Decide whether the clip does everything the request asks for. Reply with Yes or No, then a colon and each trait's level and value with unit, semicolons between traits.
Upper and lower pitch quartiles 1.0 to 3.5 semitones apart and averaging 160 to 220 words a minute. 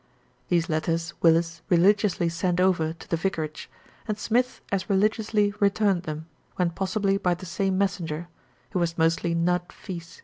No: average, 2.9 semitones; average, 150 wpm